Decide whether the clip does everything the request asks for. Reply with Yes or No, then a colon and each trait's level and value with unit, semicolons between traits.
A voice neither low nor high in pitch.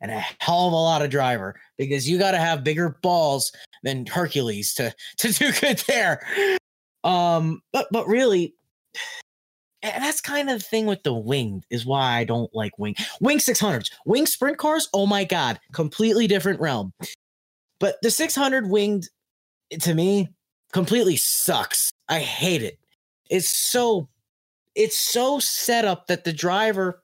Yes: medium, 180 Hz